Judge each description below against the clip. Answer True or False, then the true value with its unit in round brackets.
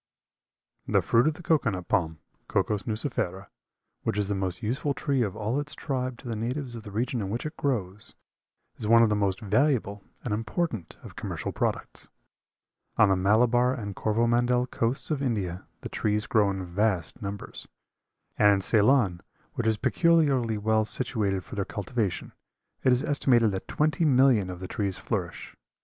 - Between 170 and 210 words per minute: True (175 wpm)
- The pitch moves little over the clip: False (4.1 semitones)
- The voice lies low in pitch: True (110 Hz)